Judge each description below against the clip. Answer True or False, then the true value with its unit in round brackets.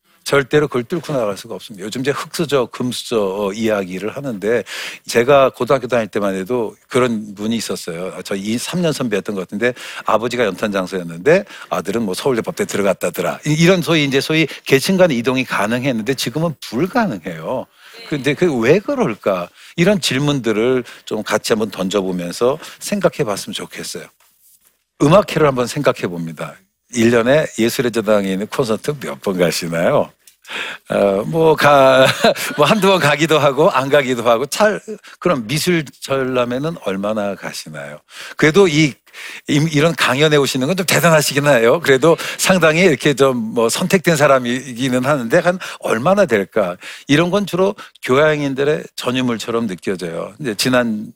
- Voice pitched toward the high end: False (135 Hz)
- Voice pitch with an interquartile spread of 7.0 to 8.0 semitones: False (5.5 semitones)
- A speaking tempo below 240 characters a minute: False (330 characters per minute)